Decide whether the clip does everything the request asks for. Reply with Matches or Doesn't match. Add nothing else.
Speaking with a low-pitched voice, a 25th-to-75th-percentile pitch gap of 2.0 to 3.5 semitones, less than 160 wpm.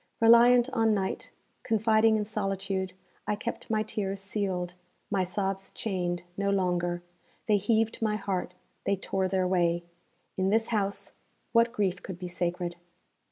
Doesn't match